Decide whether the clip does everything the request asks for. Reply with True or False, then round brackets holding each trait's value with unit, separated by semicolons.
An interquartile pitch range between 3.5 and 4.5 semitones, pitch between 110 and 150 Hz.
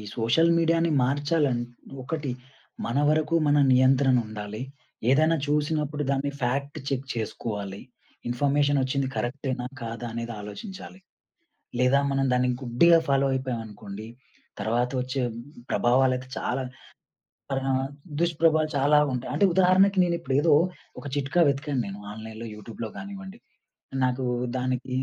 True (3.8 semitones; 135 Hz)